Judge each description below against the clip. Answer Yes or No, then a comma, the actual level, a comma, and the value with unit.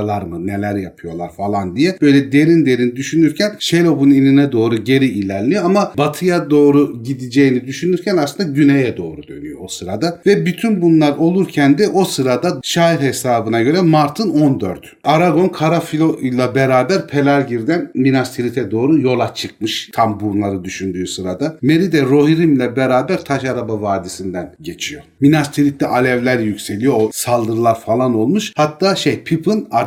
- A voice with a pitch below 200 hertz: Yes, medium, 140 Hz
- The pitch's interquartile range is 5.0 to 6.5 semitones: Yes, wide, 5.5 semitones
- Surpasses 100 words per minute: Yes, fast, 140 wpm